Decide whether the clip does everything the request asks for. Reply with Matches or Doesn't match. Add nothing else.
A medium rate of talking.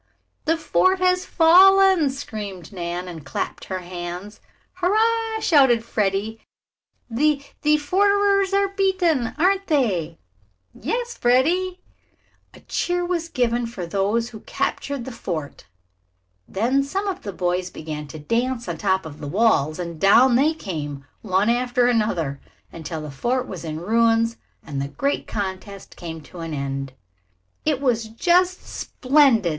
Matches